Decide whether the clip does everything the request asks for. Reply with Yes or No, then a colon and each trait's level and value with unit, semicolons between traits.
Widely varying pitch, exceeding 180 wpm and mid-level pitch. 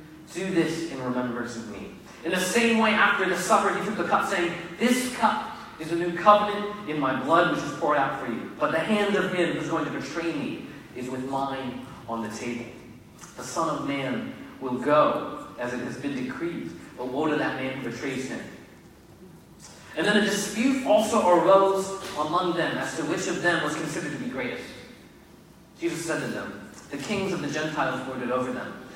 Yes: wide, 7.0 semitones; fast, 205 wpm; medium, 170 Hz